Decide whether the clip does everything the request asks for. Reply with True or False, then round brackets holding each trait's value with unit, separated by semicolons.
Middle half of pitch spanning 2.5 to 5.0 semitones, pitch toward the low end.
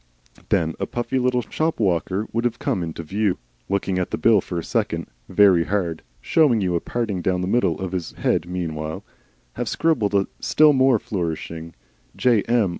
False (5.4 semitones; 95 Hz)